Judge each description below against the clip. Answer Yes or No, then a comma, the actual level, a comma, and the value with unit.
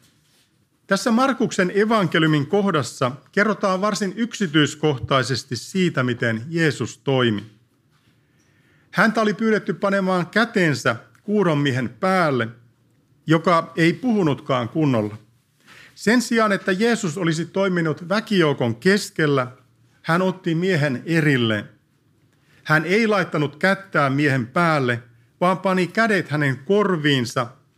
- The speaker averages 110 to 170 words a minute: No, slow, 95 wpm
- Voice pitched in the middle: Yes, medium, 155 Hz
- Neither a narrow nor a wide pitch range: No, wide, 6.5 semitones